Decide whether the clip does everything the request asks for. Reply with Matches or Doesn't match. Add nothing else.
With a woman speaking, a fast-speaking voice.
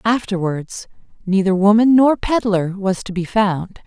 Doesn't match